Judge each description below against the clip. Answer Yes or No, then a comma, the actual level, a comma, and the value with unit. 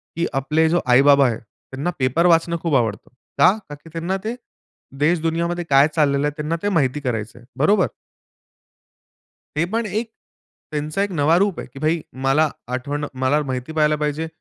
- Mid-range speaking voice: Yes, medium, 150 Hz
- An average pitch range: Yes, average, 3.7 semitones